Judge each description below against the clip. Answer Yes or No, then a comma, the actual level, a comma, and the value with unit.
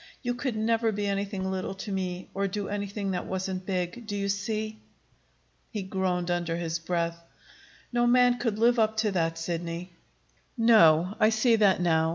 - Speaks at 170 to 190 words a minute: Yes, average, 175 wpm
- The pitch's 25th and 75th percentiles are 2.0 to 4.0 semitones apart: Yes, average, 3.5 semitones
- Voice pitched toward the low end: No, high, 195 Hz